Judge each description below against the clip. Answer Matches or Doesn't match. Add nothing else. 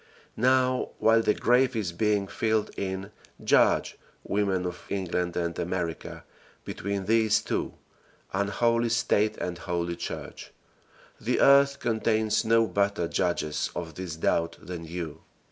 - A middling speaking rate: Doesn't match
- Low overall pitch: Matches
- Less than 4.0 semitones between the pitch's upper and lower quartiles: Doesn't match